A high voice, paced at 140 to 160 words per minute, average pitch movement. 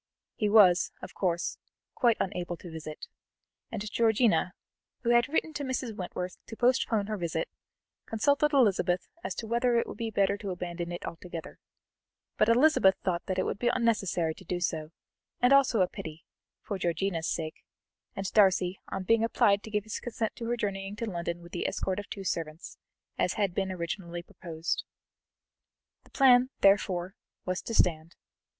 No: high, 195 Hz; average, 170 wpm; average, 4.6 semitones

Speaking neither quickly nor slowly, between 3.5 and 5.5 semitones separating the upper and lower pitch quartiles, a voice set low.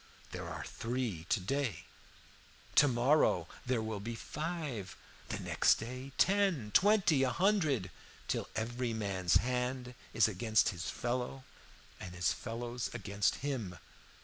No: slow, 130 wpm; average, 4.3 semitones; low, 120 Hz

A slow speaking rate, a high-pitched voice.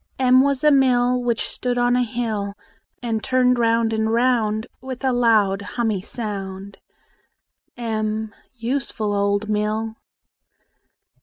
Yes: slow, 125 wpm; high, 230 Hz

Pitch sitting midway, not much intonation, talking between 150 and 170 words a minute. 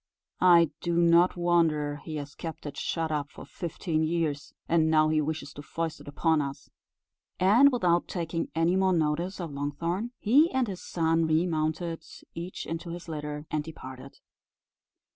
Yes: medium, 165 Hz; narrow, 2.3 semitones; average, 160 wpm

